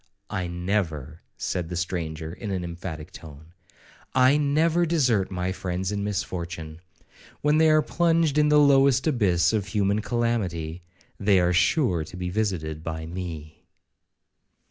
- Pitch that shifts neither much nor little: No, wide, 6.8 semitones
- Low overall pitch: Yes, very low, 95 Hz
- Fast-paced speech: No, average, 140 wpm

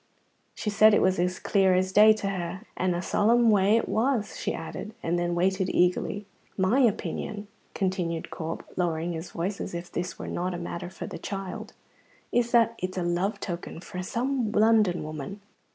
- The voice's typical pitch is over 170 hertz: Yes, high, 190 Hz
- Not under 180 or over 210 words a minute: Yes, average, 185 wpm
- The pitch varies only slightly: No, average, 3.3 semitones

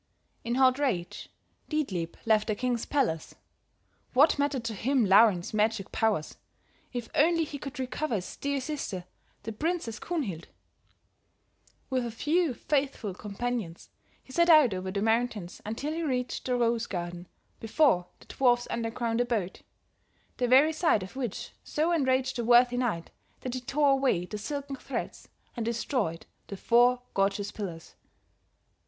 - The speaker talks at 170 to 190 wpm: No, average, 150 wpm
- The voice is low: No, high, 240 Hz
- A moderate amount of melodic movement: Yes, average, 4.7 semitones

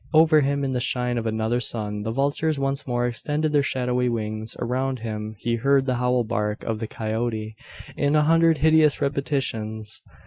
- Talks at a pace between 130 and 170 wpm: No, average, 180 wpm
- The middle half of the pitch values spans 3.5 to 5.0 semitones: Yes, average, 4.1 semitones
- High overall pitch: No, low, 125 Hz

